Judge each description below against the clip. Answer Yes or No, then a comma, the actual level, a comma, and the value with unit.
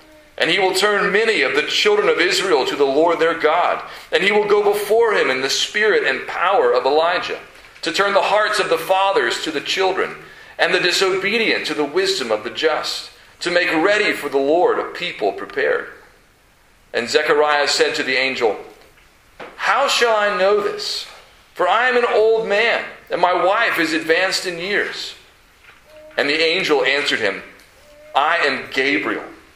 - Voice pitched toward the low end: No, high, 210 Hz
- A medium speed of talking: Yes, average, 180 wpm